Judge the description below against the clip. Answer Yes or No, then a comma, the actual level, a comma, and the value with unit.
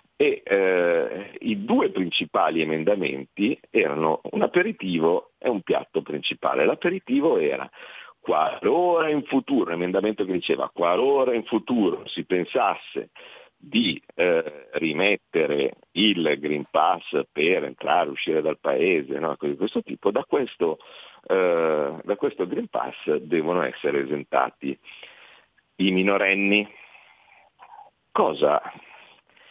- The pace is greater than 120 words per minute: No, slow, 115 wpm